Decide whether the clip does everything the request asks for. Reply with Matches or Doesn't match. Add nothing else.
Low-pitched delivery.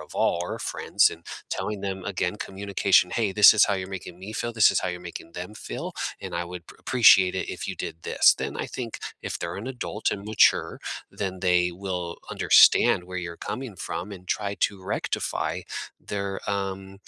Matches